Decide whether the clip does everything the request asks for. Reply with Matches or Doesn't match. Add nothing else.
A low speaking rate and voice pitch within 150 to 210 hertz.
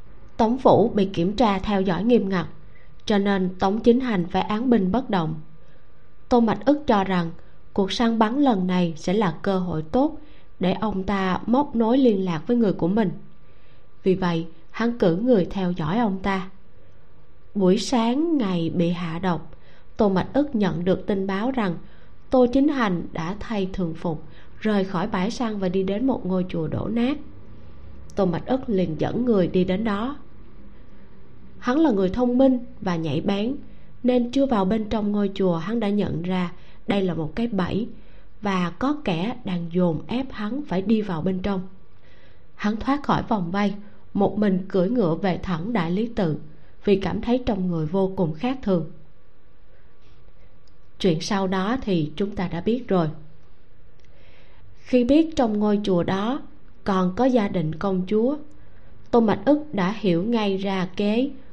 Doesn't match